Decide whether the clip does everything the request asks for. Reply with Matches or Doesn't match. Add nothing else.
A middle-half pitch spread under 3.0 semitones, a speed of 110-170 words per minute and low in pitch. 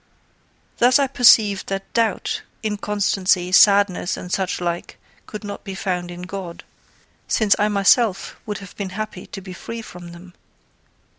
Doesn't match